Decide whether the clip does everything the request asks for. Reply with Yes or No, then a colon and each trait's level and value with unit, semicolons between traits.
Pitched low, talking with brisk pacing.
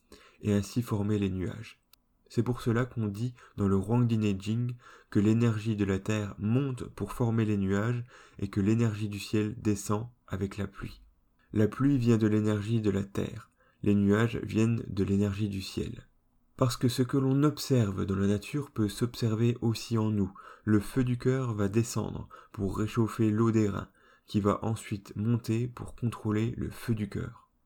No: low, 110 Hz; average, 180 wpm